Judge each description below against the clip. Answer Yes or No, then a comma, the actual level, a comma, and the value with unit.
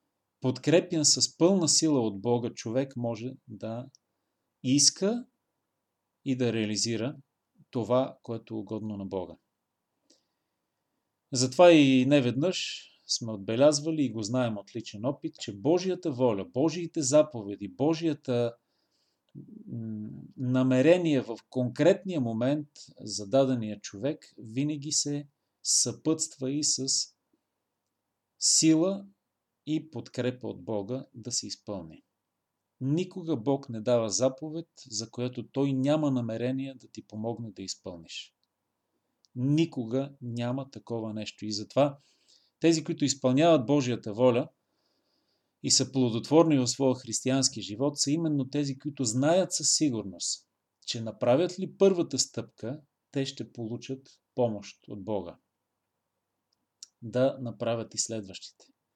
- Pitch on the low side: Yes, low, 130 Hz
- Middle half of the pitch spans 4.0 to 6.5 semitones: Yes, average, 4.5 semitones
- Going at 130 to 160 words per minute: No, slow, 115 wpm